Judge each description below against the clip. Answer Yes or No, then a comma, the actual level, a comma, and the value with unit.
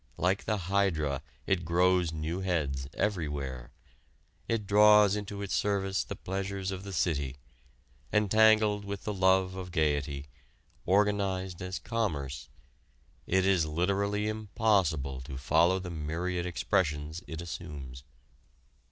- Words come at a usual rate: No, slow, 120 wpm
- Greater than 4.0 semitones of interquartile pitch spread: Yes, average, 4.5 semitones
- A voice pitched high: No, very low, 90 Hz